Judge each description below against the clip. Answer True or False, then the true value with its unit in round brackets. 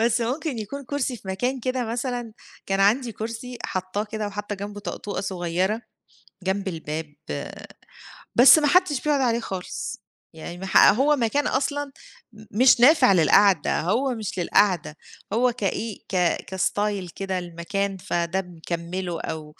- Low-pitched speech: False (205 Hz)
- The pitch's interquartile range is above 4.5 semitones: True (4.9 semitones)